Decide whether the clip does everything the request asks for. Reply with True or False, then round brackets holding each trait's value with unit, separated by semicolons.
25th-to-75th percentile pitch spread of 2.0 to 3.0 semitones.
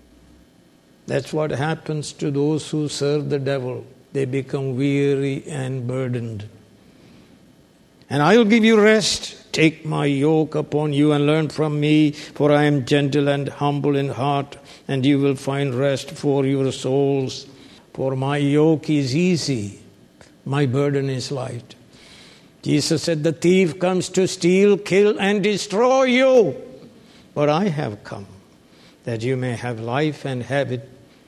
True (2.4 semitones)